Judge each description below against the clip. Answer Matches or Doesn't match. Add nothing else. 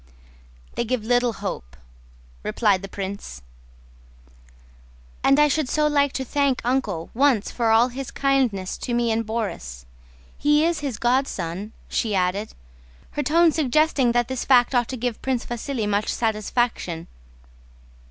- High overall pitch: Matches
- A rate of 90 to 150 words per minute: Matches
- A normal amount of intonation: Matches